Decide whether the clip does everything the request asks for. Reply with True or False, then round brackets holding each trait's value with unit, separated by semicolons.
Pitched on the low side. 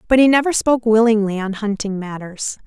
False (220 Hz)